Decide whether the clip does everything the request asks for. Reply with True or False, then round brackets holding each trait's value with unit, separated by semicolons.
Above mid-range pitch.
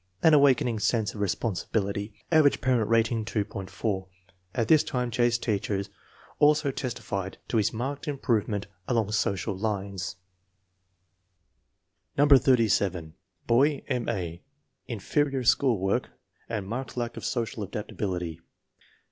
False (115 Hz)